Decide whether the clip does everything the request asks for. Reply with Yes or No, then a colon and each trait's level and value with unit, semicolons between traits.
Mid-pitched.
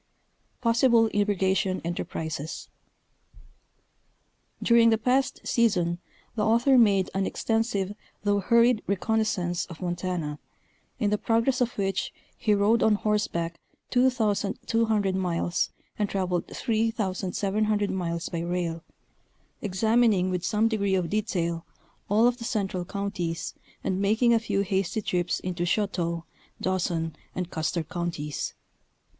No: high, 200 Hz